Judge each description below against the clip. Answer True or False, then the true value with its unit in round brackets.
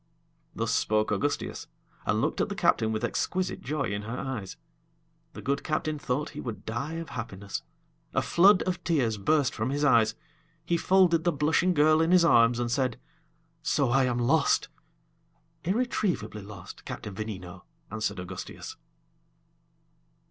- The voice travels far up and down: True (6.5 semitones)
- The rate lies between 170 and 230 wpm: False (150 wpm)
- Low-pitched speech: True (130 Hz)